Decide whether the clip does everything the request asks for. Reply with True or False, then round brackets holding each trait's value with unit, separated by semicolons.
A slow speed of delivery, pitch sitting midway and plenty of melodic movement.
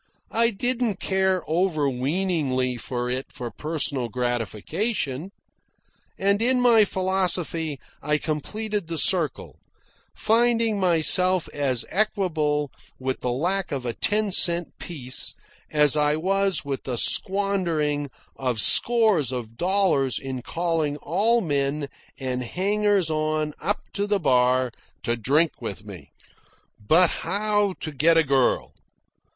True (125 wpm; 160 Hz; 6.5 semitones)